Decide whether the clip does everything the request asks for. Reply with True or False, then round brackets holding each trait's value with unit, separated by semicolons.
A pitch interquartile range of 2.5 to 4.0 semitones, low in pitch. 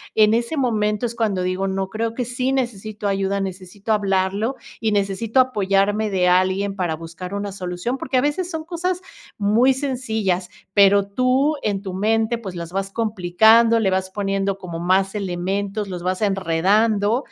False (3.2 semitones; 200 Hz)